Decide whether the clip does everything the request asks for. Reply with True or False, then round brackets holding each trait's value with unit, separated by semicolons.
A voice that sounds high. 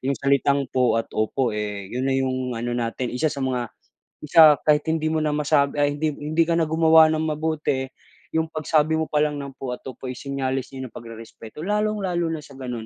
False (140 Hz)